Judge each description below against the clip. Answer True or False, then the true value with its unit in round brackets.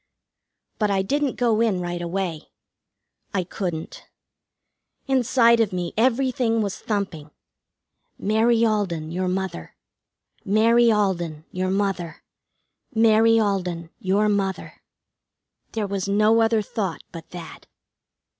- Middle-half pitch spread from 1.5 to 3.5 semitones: False (3.9 semitones)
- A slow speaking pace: True (110 wpm)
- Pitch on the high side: True (200 Hz)